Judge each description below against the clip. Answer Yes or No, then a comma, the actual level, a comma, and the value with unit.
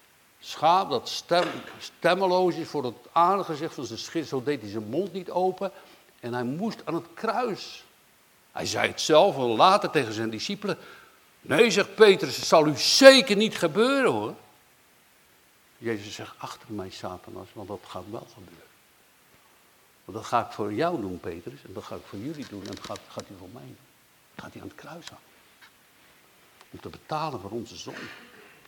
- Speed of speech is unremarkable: Yes, average, 185 wpm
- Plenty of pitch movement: Yes, wide, 8.7 semitones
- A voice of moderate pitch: Yes, medium, 165 Hz